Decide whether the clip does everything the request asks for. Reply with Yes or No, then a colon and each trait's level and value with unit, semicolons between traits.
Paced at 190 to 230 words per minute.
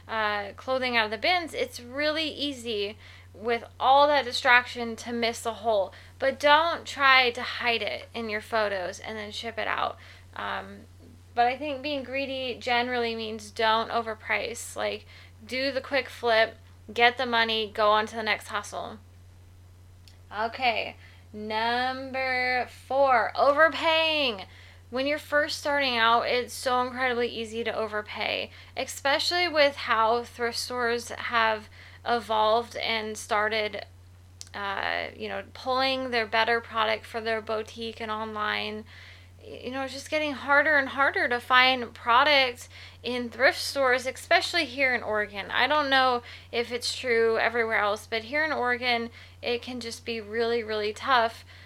No: average, 150 wpm